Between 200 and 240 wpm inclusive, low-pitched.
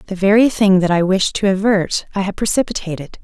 No: fast, 205 wpm; high, 195 Hz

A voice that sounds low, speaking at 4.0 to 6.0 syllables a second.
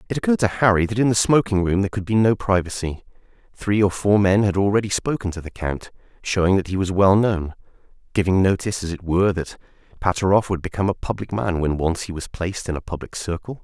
No: very low, 95 Hz; 6.4 syllables/s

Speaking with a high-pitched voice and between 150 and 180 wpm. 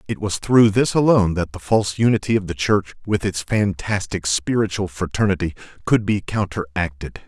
No: low, 100 Hz; average, 165 wpm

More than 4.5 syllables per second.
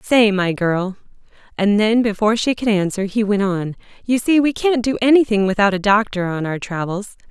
Yes: 5.2 syllables/s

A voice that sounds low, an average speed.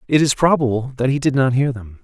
No: low, 130 Hz; fast, 265 wpm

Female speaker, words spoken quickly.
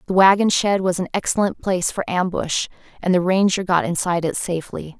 No: female; average, 190 wpm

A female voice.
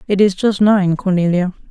Yes: female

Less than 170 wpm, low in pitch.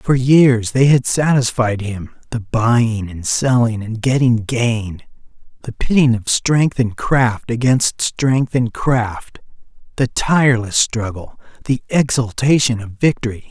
Yes: slow, 135 wpm; low, 120 Hz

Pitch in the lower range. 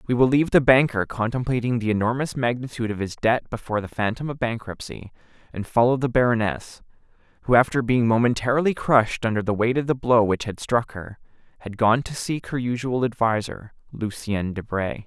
Yes: low, 115 Hz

